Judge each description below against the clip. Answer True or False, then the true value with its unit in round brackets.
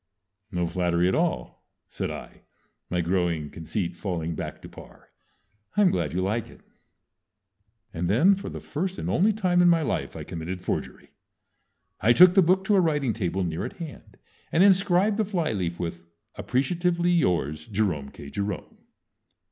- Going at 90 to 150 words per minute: False (165 wpm)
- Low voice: True (105 Hz)